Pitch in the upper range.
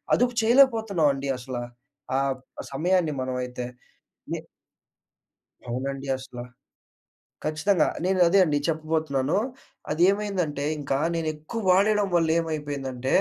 No: medium, 155 Hz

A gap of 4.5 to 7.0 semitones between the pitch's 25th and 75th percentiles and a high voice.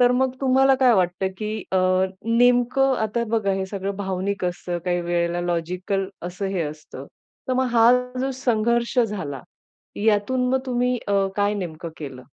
Yes: wide, 5.5 semitones; high, 205 Hz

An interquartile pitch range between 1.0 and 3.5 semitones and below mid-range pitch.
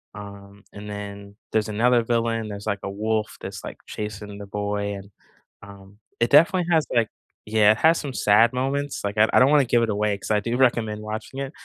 Yes: narrow, 2.6 semitones; low, 105 Hz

